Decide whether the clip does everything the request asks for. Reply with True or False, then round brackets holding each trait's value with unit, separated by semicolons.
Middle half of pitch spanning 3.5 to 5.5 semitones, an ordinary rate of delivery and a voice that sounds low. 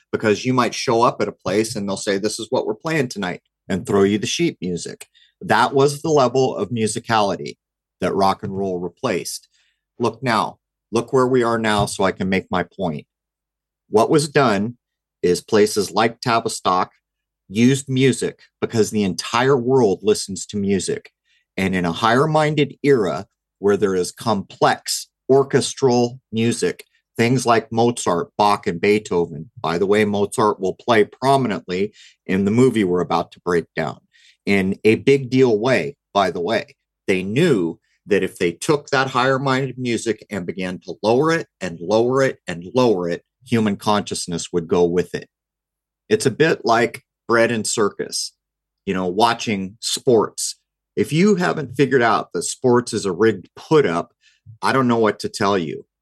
True (4.7 semitones; 170 wpm; 115 Hz)